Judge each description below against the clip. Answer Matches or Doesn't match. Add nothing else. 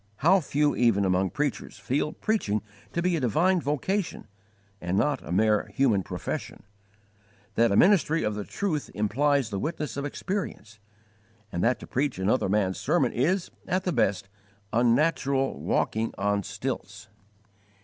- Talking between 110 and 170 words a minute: Matches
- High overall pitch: Doesn't match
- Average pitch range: Doesn't match